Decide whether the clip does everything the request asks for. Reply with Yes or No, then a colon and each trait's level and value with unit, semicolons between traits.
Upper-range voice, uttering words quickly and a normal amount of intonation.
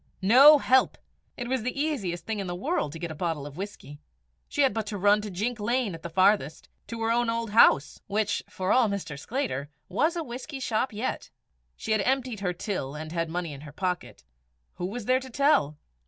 No: high, 210 Hz; fast, 215 wpm; wide, 6.2 semitones